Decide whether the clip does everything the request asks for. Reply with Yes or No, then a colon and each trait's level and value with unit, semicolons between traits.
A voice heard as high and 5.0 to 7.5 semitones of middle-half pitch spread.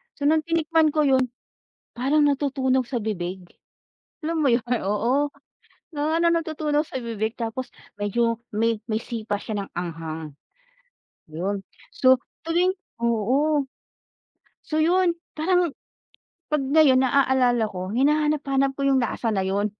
Yes: very high, 260 Hz; wide, 5.5 semitones